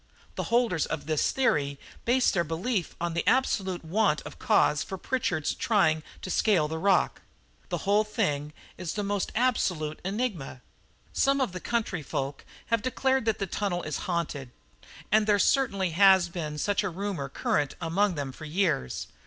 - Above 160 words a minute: Yes, average, 170 wpm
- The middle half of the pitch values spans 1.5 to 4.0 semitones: No, average, 5.3 semitones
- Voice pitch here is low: No, medium, 185 Hz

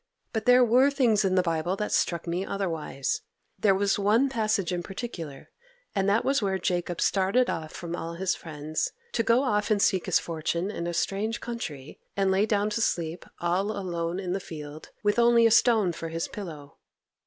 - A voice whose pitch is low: No, high, 190 Hz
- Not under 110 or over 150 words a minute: No, average, 195 wpm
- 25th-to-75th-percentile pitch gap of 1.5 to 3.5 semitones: No, average, 4.2 semitones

